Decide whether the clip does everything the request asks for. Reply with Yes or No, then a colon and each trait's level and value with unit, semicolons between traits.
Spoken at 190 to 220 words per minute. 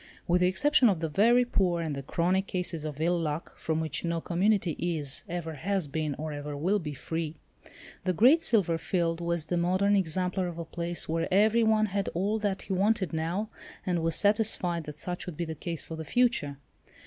Yes: fast, 205 wpm